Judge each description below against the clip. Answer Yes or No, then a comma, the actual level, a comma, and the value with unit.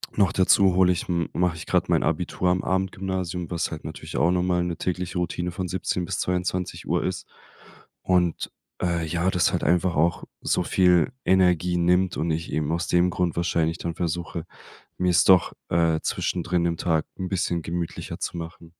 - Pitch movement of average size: No, narrow, 1.3 semitones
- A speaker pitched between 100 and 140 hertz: No, very low, 90 Hz